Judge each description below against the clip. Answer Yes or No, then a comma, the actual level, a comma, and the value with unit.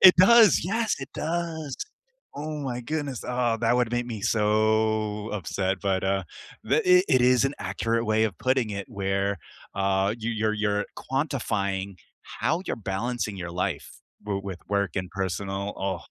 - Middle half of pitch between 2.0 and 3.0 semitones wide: No, average, 4.6 semitones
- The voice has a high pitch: No, low, 110 Hz